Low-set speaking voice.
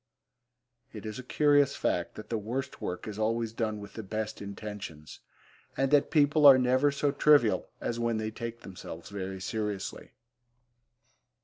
Yes: low, 110 Hz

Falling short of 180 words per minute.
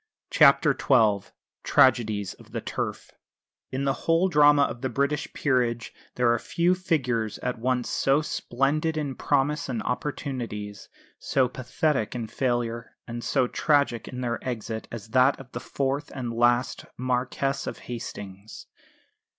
Yes: average, 140 wpm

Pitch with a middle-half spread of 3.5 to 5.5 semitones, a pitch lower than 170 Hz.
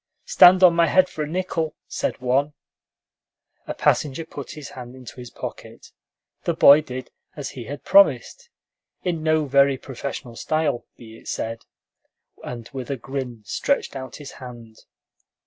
Yes: average, 4.0 semitones; medium, 140 Hz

